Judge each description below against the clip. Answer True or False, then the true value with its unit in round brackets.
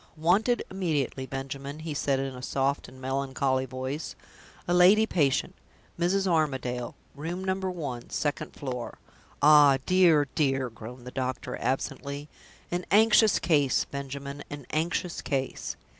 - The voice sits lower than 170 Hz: True (140 Hz)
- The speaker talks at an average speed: False (130 wpm)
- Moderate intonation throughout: True (4.4 semitones)